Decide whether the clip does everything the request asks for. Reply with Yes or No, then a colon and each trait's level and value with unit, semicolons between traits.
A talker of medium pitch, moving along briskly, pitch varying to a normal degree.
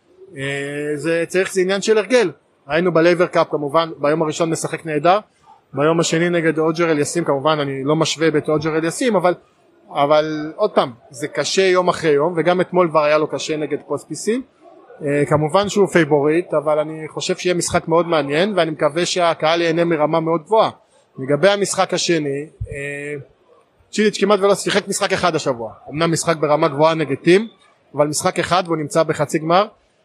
Yes: medium, 165 Hz; fast, 170 wpm; average, 3.1 semitones